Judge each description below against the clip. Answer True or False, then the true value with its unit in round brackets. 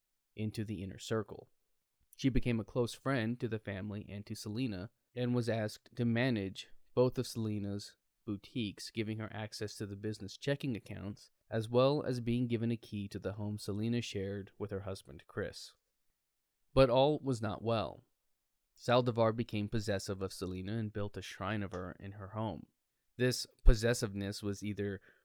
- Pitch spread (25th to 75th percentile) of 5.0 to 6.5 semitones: False (3.0 semitones)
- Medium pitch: False (110 Hz)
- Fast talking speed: False (170 wpm)